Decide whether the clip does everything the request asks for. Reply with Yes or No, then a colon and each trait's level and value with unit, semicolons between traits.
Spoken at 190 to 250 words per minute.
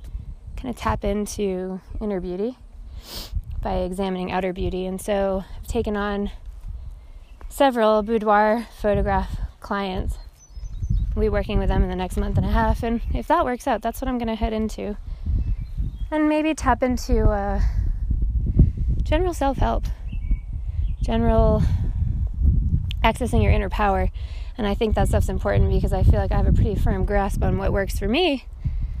No: average, 155 wpm